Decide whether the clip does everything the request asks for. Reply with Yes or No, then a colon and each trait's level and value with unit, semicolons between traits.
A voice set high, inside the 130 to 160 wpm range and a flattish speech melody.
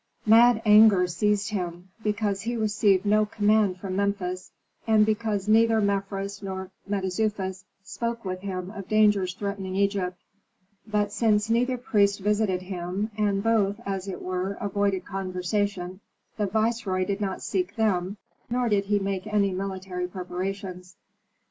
Yes: high, 200 Hz; average, 140 wpm; narrow, 2.2 semitones